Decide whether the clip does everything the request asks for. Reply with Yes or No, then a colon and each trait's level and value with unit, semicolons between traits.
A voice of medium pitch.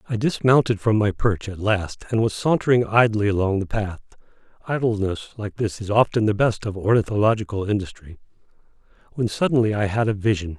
No: low, 105 Hz